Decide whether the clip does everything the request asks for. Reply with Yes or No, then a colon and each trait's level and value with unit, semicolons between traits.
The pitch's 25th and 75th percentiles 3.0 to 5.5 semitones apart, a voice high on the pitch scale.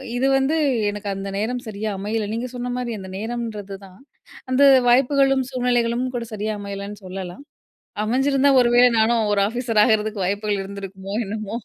Yes: average, 3.5 semitones; high, 220 Hz